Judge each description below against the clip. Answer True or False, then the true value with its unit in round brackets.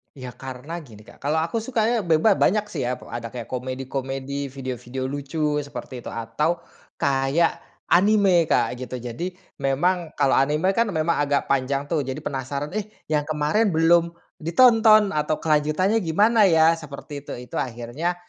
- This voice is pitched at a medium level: True (150 Hz)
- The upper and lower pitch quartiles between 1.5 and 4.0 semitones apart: False (4.6 semitones)